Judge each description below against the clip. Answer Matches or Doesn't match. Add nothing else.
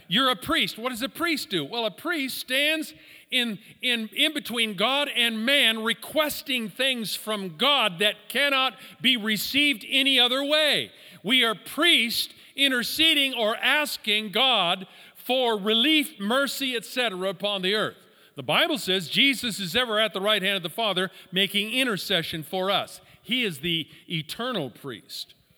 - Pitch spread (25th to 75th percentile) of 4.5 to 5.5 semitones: Matches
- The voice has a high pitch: Matches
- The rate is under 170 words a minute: Matches